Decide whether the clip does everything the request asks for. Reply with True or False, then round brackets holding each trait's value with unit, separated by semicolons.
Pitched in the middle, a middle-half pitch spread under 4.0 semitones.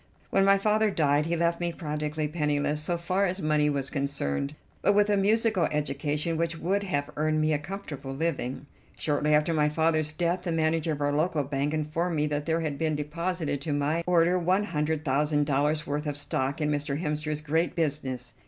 True (155 Hz; 2.4 semitones)